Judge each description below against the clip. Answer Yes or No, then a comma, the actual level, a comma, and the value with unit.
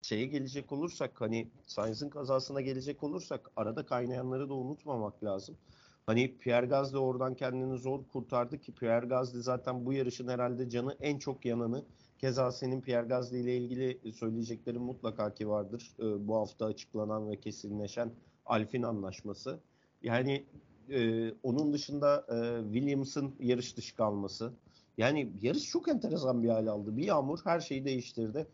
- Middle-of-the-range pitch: No, low, 125 Hz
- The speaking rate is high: Yes, fast, 145 wpm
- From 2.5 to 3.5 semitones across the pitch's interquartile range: Yes, average, 2.9 semitones